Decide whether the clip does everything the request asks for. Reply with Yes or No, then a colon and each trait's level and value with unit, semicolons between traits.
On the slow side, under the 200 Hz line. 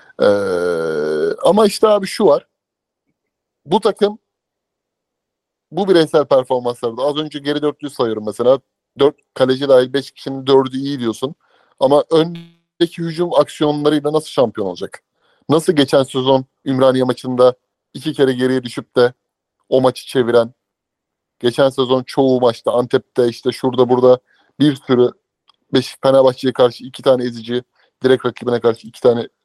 No: average, 135 wpm; low, 135 Hz